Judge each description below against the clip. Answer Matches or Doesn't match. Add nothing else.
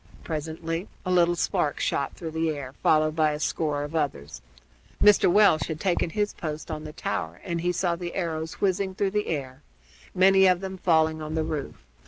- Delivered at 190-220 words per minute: Matches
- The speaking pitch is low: Doesn't match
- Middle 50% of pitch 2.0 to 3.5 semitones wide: Matches